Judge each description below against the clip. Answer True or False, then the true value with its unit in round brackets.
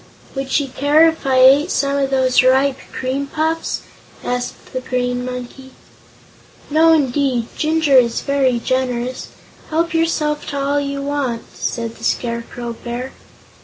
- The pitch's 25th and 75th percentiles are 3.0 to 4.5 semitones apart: False (2.5 semitones)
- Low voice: False (270 Hz)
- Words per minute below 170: True (140 wpm)